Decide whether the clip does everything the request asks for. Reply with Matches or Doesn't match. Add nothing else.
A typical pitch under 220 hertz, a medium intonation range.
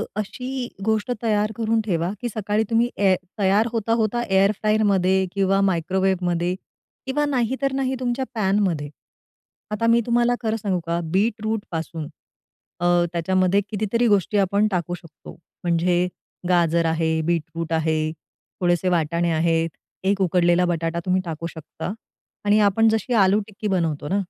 Matches